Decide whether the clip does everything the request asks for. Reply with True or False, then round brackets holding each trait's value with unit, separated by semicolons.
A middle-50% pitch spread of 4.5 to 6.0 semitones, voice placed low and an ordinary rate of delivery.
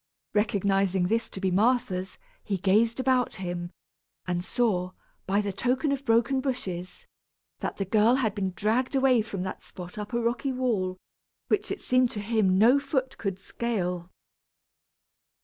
False (4.8 semitones; 215 Hz; 155 wpm)